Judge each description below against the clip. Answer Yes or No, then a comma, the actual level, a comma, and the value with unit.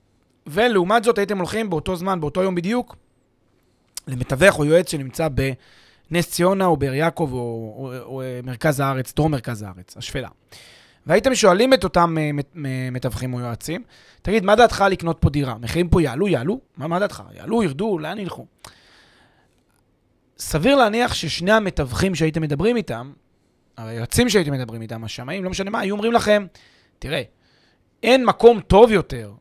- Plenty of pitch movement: Yes, wide, 7.5 semitones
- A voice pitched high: No, medium, 160 Hz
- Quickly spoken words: Yes, fast, 155 wpm